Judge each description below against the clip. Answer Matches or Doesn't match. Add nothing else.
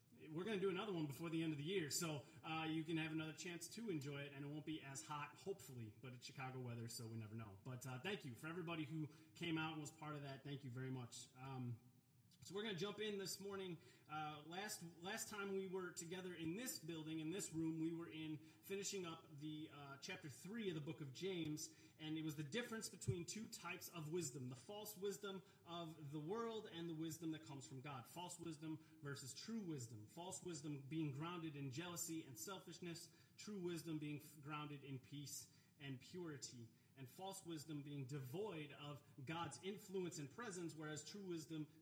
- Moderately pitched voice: Matches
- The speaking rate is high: Matches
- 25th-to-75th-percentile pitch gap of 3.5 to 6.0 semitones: Matches